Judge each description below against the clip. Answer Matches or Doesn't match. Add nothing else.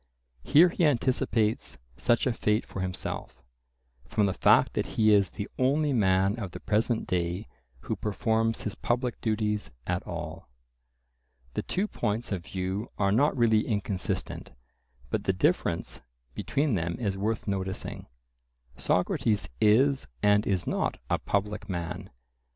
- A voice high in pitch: Doesn't match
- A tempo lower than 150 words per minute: Matches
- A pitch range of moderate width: Matches